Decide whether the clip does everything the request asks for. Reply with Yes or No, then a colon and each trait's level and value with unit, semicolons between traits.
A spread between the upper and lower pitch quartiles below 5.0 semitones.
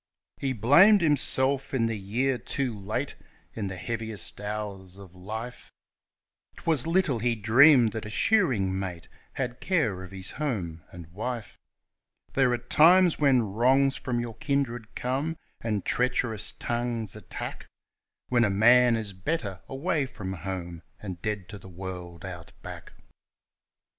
No: wide, 5.4 semitones